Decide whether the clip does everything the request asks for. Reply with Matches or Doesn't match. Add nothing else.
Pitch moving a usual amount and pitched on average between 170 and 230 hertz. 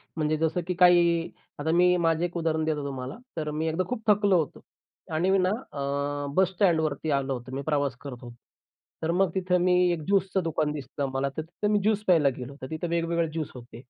Doesn't match